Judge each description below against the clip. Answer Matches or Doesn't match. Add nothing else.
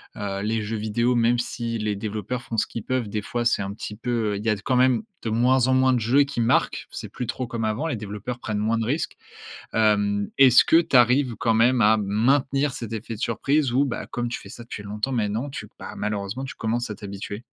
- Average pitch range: Matches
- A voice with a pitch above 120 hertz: Doesn't match